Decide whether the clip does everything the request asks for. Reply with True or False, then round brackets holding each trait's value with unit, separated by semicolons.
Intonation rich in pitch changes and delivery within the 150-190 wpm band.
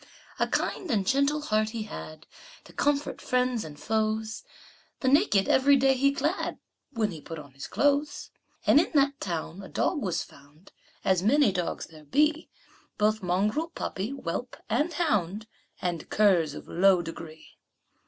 True (8.0 semitones; 160 wpm)